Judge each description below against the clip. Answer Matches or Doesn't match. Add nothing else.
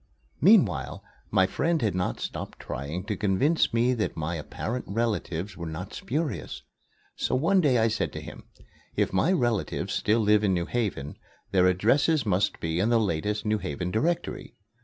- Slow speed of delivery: Doesn't match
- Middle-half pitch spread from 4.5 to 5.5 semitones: Matches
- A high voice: Doesn't match